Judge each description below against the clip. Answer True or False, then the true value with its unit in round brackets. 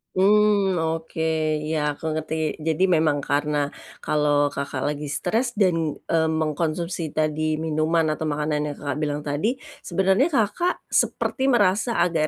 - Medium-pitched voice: True (160 Hz)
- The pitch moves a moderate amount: True (3.6 semitones)